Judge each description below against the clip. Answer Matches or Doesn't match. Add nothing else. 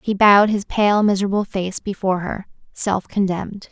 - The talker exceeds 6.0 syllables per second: Doesn't match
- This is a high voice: Matches